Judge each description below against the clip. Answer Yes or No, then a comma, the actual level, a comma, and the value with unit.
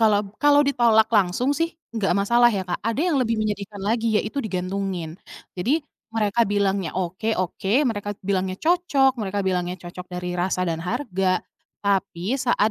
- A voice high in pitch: Yes, high, 205 Hz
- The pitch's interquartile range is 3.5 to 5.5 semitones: Yes, average, 4.1 semitones